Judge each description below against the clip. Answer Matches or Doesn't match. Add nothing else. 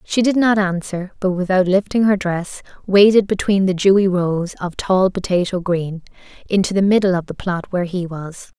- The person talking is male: Doesn't match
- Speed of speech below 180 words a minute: Doesn't match